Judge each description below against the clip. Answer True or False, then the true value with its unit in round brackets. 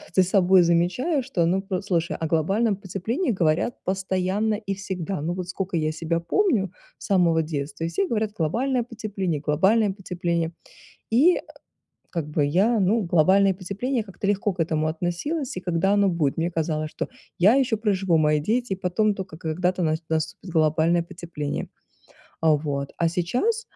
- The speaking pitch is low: False (185 Hz)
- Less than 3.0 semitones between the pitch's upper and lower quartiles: False (3.9 semitones)